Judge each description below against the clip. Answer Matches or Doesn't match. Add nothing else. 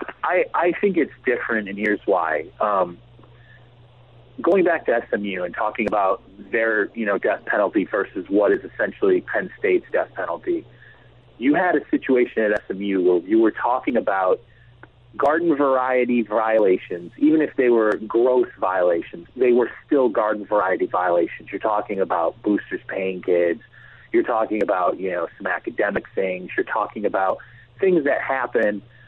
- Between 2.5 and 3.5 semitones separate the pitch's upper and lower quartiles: Doesn't match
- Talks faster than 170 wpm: Doesn't match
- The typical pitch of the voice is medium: Doesn't match